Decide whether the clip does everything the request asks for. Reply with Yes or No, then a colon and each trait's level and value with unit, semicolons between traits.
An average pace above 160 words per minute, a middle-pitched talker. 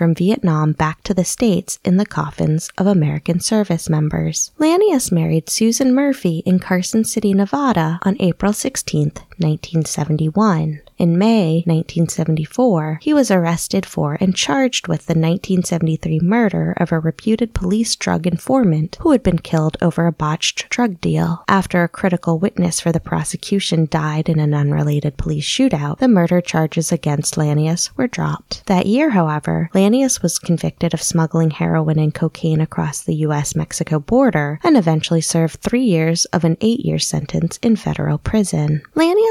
No: average, 155 wpm; medium, 170 Hz